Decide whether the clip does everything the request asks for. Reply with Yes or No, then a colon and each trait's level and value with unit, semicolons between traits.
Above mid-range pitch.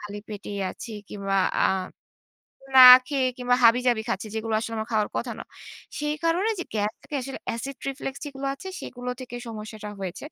Yes: high, 235 Hz